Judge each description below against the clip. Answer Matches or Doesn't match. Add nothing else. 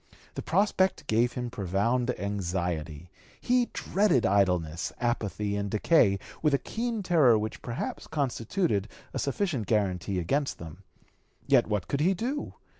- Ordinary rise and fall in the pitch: Doesn't match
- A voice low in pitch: Matches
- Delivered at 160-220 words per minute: Doesn't match